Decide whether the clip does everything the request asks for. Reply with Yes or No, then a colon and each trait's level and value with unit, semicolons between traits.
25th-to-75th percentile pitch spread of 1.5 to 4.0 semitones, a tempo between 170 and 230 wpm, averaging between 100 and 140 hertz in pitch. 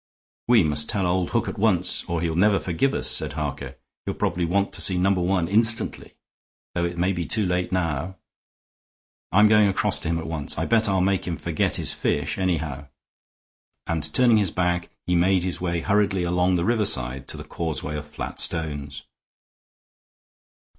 No: average, 3.1 semitones; average, 180 wpm; very low, 90 Hz